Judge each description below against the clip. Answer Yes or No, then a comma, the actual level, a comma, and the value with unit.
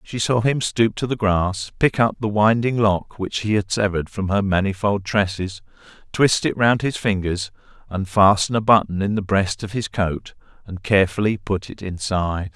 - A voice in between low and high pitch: No, low, 100 Hz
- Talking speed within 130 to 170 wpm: No, average, 185 wpm